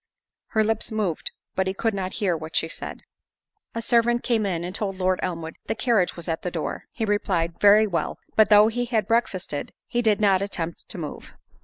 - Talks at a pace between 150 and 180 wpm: No, fast, 205 wpm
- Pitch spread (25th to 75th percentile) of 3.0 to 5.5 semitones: Yes, average, 3.9 semitones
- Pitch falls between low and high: No, high, 200 Hz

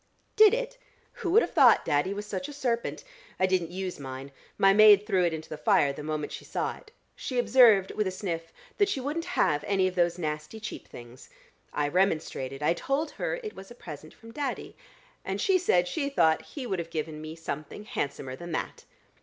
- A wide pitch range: Yes, wide, 7.7 semitones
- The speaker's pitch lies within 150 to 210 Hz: Yes, medium, 185 Hz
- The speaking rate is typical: No, fast, 210 wpm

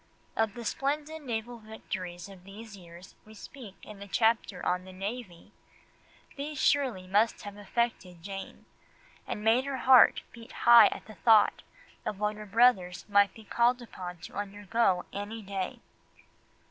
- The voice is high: Yes, high, 210 Hz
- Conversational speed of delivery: Yes, average, 155 wpm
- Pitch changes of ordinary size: Yes, average, 3.6 semitones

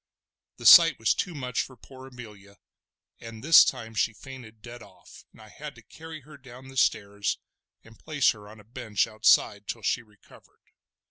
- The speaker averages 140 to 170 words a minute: No, average, 185 wpm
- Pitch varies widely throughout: No, average, 3.8 semitones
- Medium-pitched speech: No, low, 115 Hz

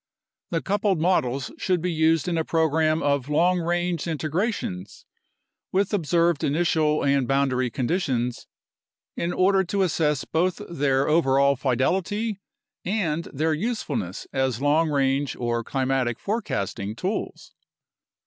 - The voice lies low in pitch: No, medium, 155 Hz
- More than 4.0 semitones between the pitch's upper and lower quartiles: Yes, average, 4.6 semitones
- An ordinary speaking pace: No, slow, 120 wpm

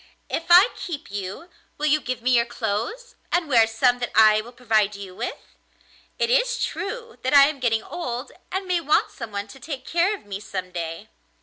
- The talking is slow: No, average, 200 wpm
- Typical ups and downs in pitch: No, wide, 7.8 semitones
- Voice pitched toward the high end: Yes, very high, 250 Hz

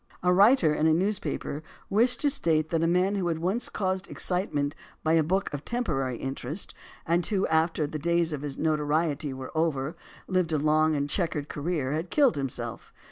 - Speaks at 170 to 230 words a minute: Yes, average, 190 wpm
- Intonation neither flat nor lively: Yes, average, 3.8 semitones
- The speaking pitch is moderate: Yes, medium, 160 Hz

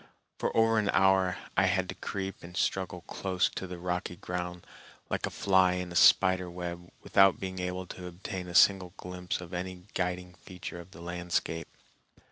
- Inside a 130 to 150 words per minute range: No, average, 180 wpm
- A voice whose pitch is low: Yes, very low, 90 Hz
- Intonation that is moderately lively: No, narrow, 1.1 semitones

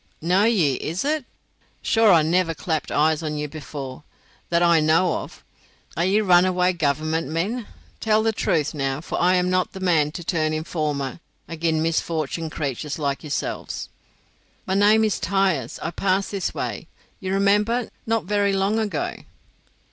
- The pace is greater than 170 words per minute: No, average, 165 wpm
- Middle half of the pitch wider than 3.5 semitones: Yes, average, 4.0 semitones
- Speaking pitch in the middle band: Yes, medium, 170 Hz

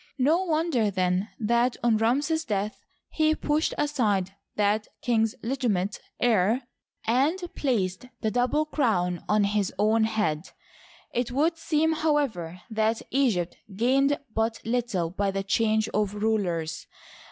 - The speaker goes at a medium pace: No, slow, 130 wpm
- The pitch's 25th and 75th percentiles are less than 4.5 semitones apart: No, average, 5.1 semitones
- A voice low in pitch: No, high, 225 Hz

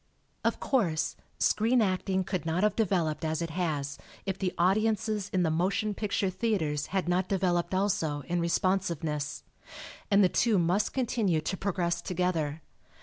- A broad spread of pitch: No, average, 3.4 semitones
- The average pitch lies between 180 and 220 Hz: Yes, medium, 185 Hz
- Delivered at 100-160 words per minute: Yes, average, 150 wpm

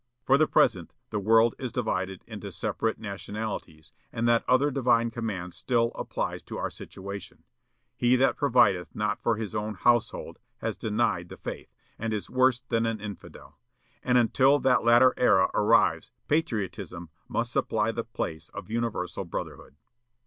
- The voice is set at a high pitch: No, low, 115 Hz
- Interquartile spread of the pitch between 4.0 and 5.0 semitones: No, average, 3.5 semitones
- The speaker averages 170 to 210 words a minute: No, average, 155 wpm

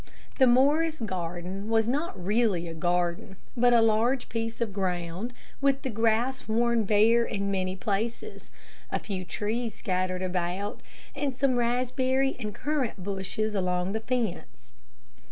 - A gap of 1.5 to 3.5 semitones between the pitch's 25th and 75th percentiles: No, average, 4.5 semitones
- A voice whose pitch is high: Yes, high, 220 Hz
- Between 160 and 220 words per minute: No, average, 140 wpm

